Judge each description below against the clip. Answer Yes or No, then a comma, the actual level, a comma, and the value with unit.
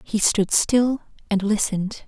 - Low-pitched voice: No, high, 210 Hz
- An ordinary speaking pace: Yes, average, 145 wpm